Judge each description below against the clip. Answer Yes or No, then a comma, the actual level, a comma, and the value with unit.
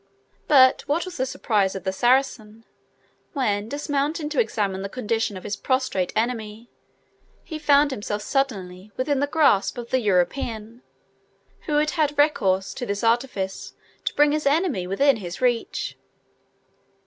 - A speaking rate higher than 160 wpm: No, average, 150 wpm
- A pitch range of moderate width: No, wide, 5.7 semitones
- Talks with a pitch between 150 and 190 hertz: No, high, 240 Hz